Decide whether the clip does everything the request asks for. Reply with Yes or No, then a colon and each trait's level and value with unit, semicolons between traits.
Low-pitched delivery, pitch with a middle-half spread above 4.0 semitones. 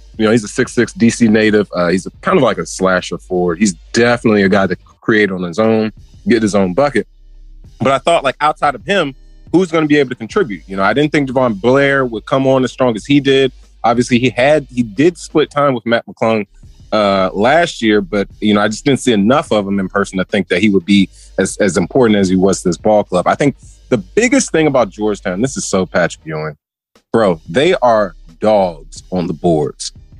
Yes: low, 110 Hz; average, 5.1 semitones